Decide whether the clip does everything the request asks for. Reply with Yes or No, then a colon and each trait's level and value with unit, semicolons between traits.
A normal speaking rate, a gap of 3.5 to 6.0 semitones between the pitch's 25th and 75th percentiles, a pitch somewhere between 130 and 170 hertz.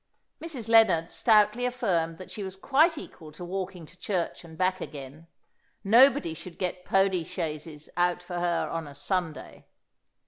No: average, 160 wpm; average, 4.1 semitones; medium, 180 Hz